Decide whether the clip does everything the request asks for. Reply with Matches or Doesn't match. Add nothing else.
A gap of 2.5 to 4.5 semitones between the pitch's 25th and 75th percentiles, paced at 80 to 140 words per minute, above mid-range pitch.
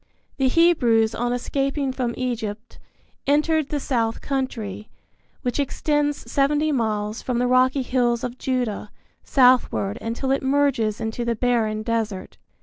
Matches